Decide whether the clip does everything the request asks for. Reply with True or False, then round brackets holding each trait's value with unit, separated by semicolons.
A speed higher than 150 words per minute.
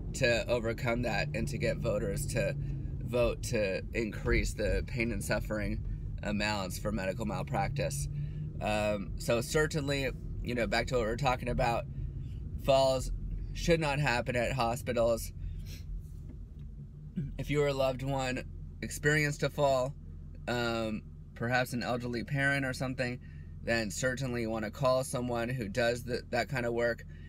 False (145 wpm)